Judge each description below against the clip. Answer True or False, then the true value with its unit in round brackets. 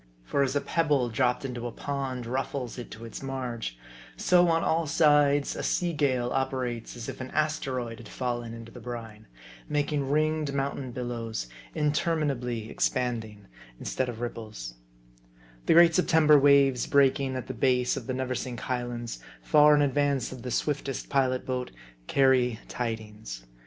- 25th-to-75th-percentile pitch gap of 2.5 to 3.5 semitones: True (3.0 semitones)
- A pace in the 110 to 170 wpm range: True (155 wpm)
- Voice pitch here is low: True (130 Hz)